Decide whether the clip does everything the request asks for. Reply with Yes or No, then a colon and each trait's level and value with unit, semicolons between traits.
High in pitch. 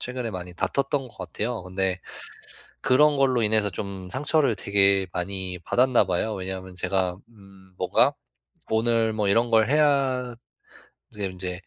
No: low, 105 Hz